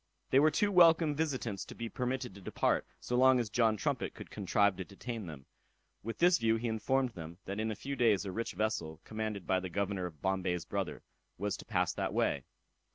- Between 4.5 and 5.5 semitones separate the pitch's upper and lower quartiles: Yes, average, 4.8 semitones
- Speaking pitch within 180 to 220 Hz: No, low, 110 Hz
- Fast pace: Yes, fast, 215 wpm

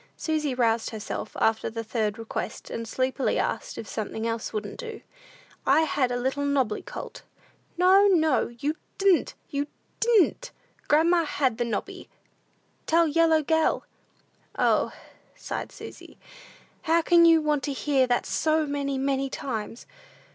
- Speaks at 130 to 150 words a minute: Yes, average, 140 wpm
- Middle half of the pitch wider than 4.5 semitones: Yes, average, 5.1 semitones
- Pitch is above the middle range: Yes, very high, 280 Hz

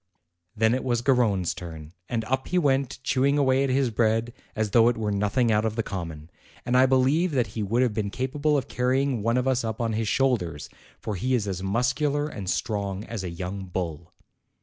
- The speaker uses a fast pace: Yes, fast, 215 wpm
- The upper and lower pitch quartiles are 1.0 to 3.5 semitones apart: No, average, 4.5 semitones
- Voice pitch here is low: Yes, low, 115 Hz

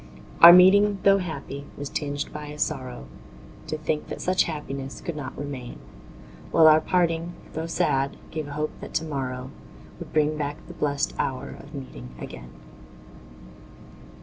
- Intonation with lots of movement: No, average, 2.9 semitones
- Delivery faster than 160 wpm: No, average, 155 wpm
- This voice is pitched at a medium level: Yes, medium, 150 Hz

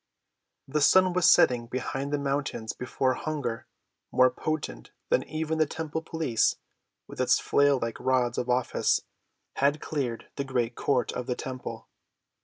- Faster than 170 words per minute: No, average, 145 wpm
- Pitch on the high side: No, low, 135 Hz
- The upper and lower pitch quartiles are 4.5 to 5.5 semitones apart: No, average, 3.6 semitones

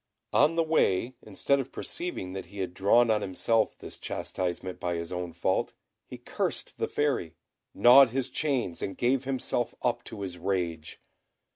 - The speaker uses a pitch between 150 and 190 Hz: No, low, 105 Hz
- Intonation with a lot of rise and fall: Yes, wide, 6.4 semitones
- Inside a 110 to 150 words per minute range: No, average, 165 wpm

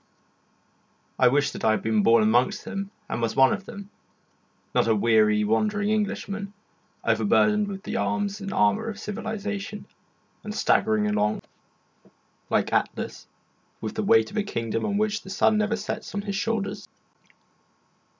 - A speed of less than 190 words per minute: Yes, average, 155 wpm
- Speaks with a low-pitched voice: No, high, 200 Hz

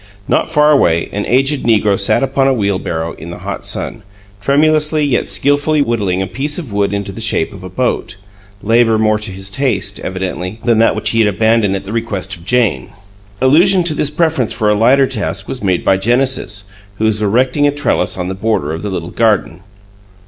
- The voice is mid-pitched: No, low, 110 Hz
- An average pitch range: No, wide, 5.7 semitones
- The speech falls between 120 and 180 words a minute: No, fast, 205 wpm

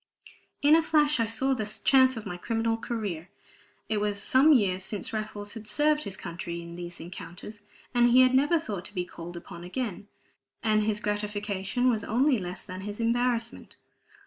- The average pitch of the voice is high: Yes, high, 215 Hz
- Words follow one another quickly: No, average, 175 wpm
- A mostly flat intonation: No, average, 4.6 semitones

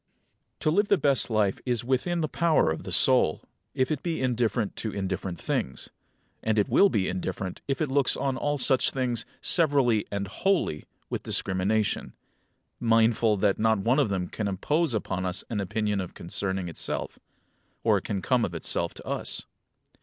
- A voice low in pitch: Yes, low, 110 Hz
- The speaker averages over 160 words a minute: Yes, average, 175 wpm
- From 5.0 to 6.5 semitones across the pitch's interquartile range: Yes, wide, 5.6 semitones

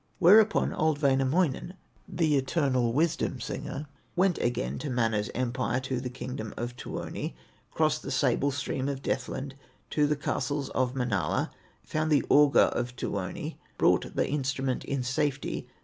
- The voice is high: No, low, 135 Hz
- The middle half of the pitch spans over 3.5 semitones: No, average, 3.1 semitones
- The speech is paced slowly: No, average, 145 wpm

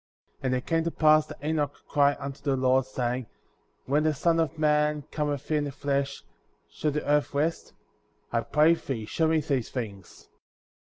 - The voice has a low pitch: No, medium, 145 Hz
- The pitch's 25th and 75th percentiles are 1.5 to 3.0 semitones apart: Yes, narrow, 2.5 semitones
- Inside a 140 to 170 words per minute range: No, average, 185 wpm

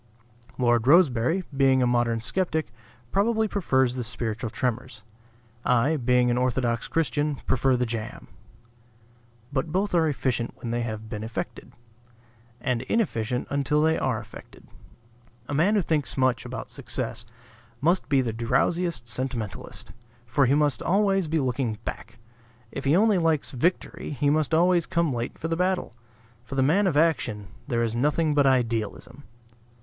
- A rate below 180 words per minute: Yes, average, 155 wpm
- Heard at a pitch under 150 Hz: Yes, low, 135 Hz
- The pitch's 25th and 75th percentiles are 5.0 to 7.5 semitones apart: Yes, average, 5.3 semitones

